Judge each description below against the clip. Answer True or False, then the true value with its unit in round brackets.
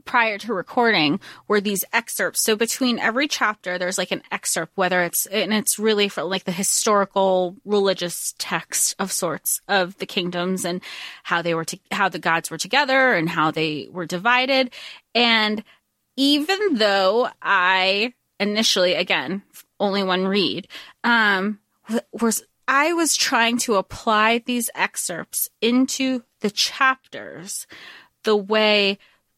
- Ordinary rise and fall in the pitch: True (4.3 semitones)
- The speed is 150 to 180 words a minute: False (140 wpm)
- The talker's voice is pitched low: False (210 Hz)